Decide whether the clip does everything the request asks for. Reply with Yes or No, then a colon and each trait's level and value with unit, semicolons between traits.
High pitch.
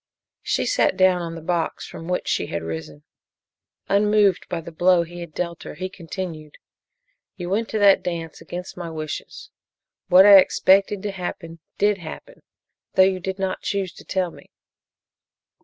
No: medium, 180 Hz